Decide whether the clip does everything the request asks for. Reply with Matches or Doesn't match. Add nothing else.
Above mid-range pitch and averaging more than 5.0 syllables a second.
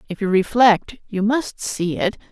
Doesn't match